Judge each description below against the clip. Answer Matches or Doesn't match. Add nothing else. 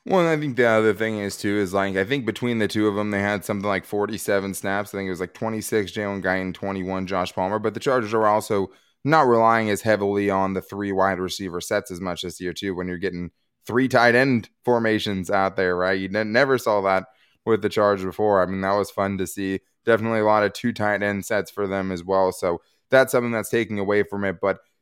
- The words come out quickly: Matches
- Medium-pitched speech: Doesn't match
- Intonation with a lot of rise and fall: Doesn't match